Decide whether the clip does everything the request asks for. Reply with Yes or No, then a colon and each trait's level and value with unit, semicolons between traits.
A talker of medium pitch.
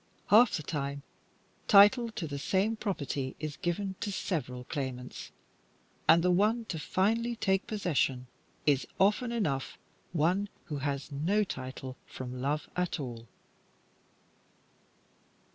Yes: medium, 165 Hz